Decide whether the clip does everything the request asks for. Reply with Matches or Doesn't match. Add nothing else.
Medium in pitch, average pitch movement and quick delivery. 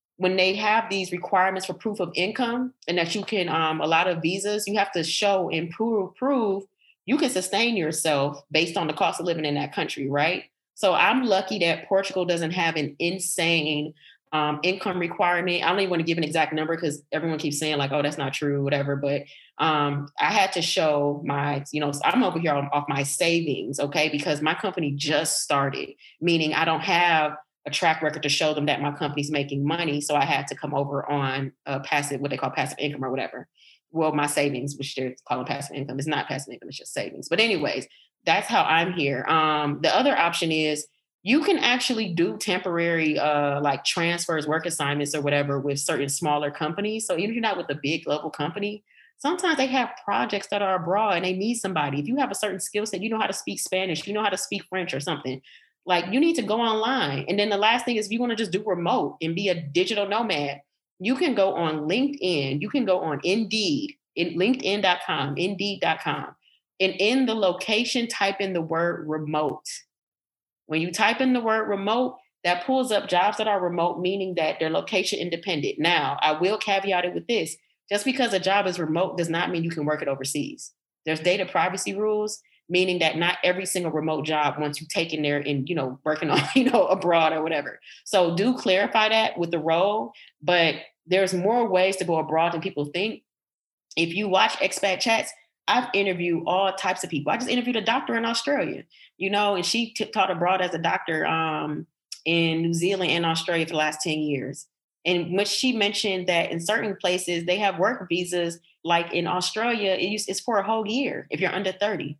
Matches